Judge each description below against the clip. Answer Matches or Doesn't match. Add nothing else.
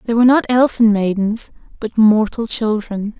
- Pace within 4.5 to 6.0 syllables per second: Matches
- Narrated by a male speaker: Doesn't match